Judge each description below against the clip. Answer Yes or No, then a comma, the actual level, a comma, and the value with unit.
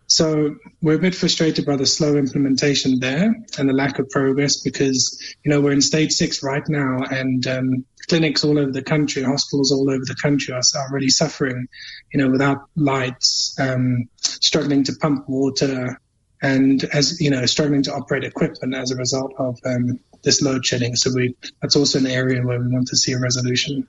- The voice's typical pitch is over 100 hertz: Yes, low, 135 Hz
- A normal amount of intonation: No, narrow, 2.0 semitones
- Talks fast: No, average, 195 wpm